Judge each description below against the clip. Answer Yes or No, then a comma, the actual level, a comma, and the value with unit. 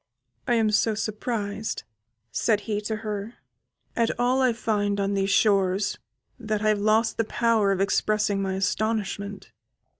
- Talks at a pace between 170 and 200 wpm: No, average, 150 wpm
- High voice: Yes, high, 210 Hz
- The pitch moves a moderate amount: No, narrow, 1.8 semitones